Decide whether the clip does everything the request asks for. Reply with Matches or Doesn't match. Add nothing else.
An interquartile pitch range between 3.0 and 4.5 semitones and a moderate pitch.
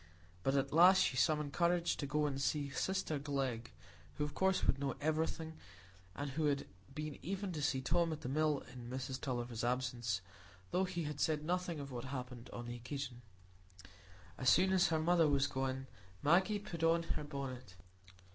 Matches